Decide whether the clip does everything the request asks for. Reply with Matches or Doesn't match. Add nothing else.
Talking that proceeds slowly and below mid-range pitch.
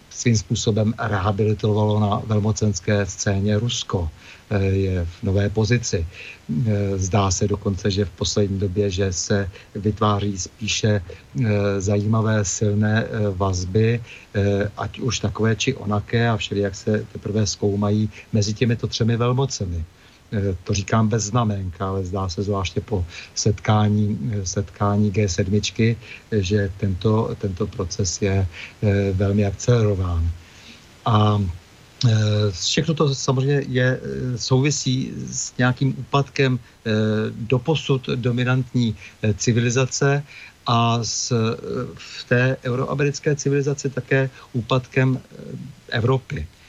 Matches